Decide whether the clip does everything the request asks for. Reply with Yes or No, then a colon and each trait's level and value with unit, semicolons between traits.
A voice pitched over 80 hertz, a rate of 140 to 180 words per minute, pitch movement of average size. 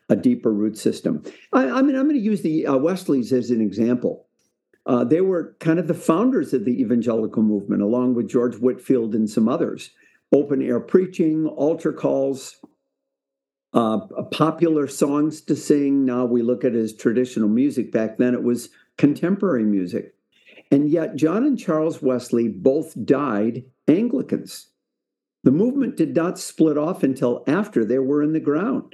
Yes: low, 135 Hz; average, 170 wpm; average, 5.0 semitones